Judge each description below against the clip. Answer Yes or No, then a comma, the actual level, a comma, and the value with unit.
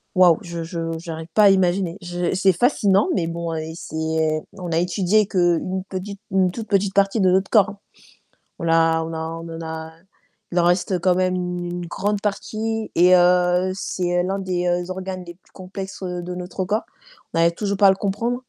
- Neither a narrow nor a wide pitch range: No, narrow, 2.2 semitones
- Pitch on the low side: No, medium, 180 Hz